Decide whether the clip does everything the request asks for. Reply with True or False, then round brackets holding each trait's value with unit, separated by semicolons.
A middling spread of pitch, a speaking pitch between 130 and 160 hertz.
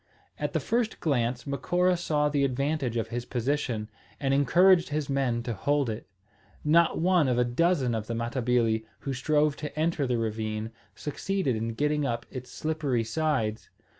True (4.5 semitones; 135 Hz)